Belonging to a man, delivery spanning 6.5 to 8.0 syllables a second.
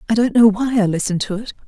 No: female; 7.1 syllables/s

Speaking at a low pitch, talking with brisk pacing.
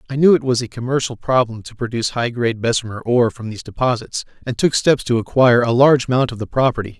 Yes: low, 120 Hz; fast, 230 wpm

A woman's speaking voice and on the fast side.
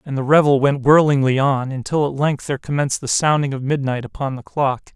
No: male; fast, 220 wpm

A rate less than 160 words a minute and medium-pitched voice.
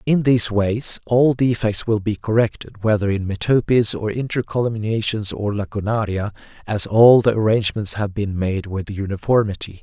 No: average, 145 wpm; low, 110 Hz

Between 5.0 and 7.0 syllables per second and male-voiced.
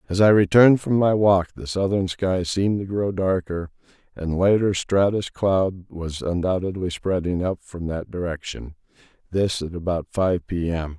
No: 4.6 syllables/s; male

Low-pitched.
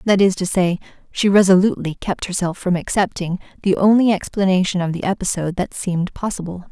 No: medium, 185 Hz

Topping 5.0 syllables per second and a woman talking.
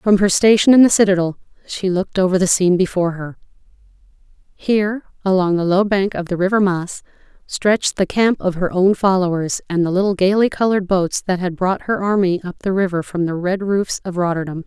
Yes: 5.7 syllables/s; female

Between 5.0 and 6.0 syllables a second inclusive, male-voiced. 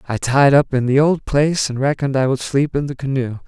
Yes: 5.8 syllables/s; male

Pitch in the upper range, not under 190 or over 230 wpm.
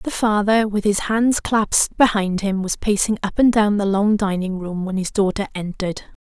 Yes: high, 205 Hz; average, 200 wpm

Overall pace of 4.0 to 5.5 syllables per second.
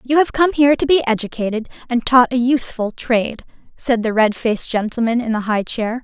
No: 5.8 syllables/s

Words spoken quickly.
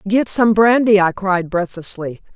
No: average, 155 wpm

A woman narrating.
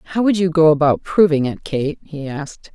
Yes: female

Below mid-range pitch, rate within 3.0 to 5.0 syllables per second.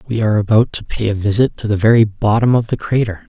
No: low, 110 Hz; 6.4 syllables/s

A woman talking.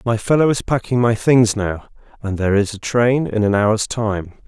No: male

